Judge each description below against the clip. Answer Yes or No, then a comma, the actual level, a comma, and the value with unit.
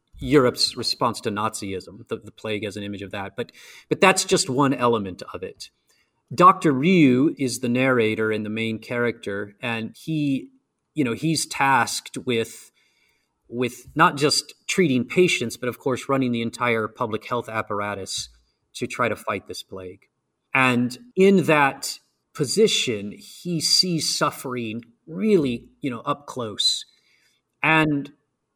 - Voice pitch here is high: No, low, 125 Hz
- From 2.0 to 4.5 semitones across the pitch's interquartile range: No, average, 4.9 semitones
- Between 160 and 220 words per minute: No, average, 145 wpm